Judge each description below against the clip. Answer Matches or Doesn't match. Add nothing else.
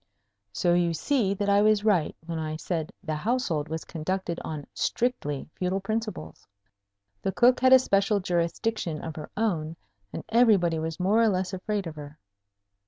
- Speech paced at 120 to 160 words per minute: Doesn't match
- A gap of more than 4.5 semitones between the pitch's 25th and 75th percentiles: Matches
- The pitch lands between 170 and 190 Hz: Matches